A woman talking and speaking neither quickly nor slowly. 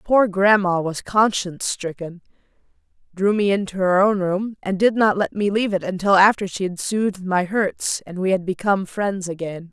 Yes: female; average, 190 wpm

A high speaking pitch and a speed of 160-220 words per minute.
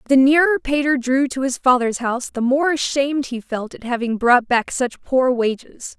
Yes: very high, 260 Hz; average, 200 wpm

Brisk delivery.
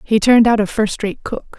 Yes: fast, 265 wpm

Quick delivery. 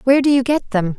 Yes: fast, 305 wpm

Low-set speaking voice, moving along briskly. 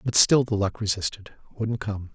No: low, 105 Hz; average, 195 wpm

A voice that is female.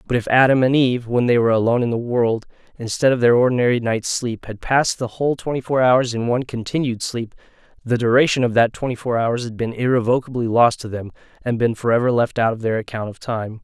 No: male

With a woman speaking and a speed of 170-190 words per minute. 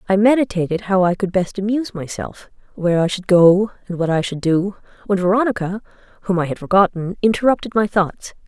Yes: female; average, 185 wpm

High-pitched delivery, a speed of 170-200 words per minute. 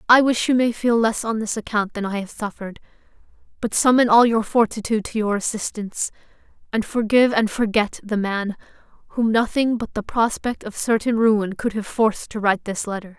Yes: high, 220 Hz; average, 190 wpm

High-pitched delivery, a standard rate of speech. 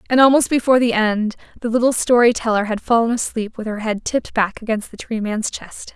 No: high, 225 Hz; fast, 220 wpm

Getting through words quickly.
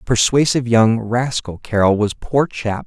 No: slow, 125 wpm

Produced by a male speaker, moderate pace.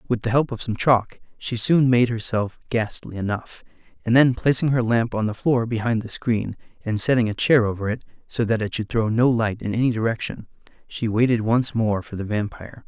No: male; fast, 215 wpm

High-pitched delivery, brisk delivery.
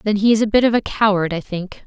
Yes: high, 205 Hz; fast, 320 wpm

